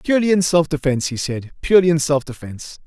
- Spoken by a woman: No, male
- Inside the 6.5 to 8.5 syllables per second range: Yes, 7.0 syllables/s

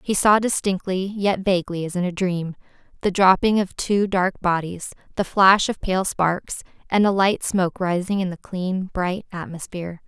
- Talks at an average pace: Yes, average, 180 wpm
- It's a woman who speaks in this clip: Yes, female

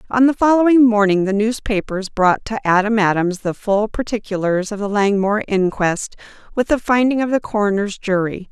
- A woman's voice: Yes, female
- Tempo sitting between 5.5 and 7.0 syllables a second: No, 5.2 syllables/s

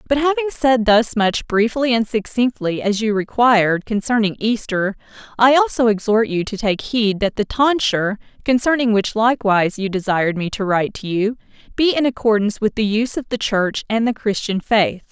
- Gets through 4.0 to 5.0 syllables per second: No, 5.3 syllables/s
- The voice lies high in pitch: Yes, high, 220 Hz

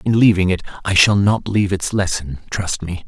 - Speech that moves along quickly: Yes, fast, 215 wpm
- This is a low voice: Yes, very low, 95 Hz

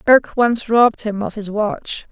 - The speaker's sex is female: Yes, female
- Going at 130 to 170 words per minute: No, average, 200 wpm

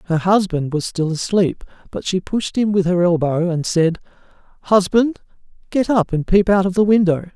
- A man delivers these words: Yes, male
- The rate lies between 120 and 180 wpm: No, average, 190 wpm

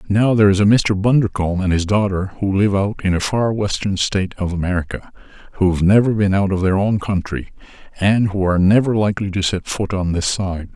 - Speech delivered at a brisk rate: Yes, fast, 210 wpm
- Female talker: No, male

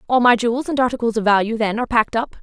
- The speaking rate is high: Yes, fast, 275 wpm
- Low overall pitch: No, high, 235 Hz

